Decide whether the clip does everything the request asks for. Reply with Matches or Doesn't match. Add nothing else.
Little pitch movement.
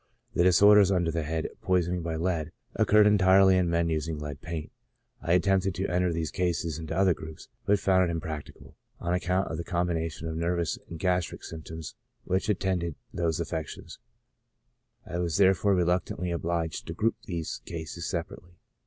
Matches